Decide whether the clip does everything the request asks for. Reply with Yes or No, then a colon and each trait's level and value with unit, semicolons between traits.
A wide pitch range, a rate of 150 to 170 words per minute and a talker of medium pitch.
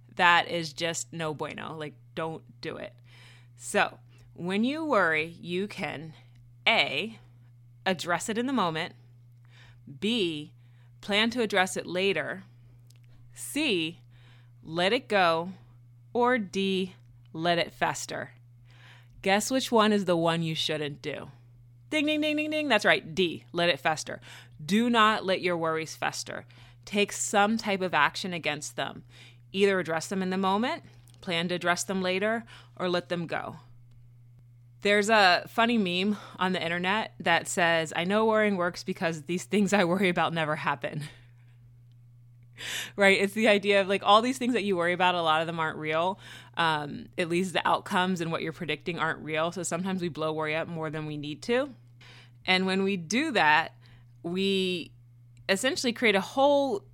Yes: wide, 8.0 semitones; average, 165 wpm; medium, 165 Hz